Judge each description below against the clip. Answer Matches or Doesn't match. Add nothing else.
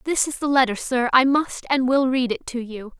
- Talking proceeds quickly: Matches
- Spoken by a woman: Matches